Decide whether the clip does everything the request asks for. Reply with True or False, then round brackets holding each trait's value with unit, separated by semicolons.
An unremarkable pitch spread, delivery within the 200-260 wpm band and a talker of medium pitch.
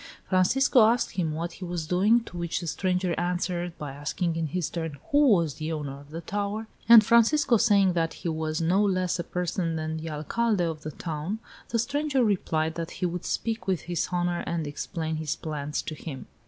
True (4.1 semitones; 205 wpm; 175 Hz)